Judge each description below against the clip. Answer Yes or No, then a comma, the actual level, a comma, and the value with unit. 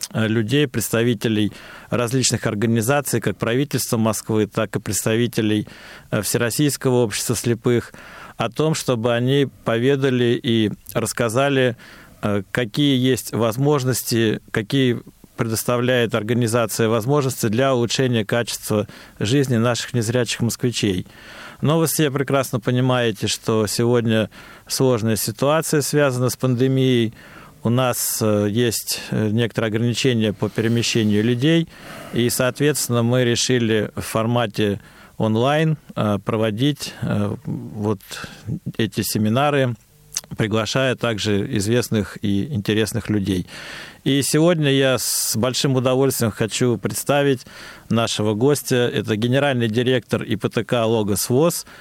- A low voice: Yes, low, 120 Hz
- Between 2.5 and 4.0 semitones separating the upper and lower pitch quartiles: Yes, average, 2.9 semitones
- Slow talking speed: Yes, slow, 100 wpm